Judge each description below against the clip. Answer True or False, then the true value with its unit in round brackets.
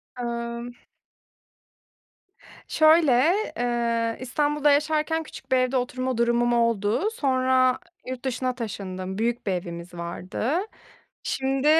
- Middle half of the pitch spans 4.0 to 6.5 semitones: False (2.5 semitones)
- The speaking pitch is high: True (245 Hz)